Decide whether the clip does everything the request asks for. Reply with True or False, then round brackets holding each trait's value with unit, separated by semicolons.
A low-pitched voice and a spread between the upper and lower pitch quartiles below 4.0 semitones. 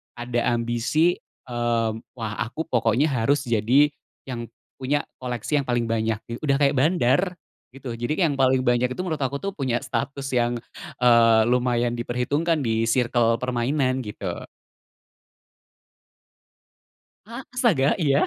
True (125 Hz; 3.0 semitones)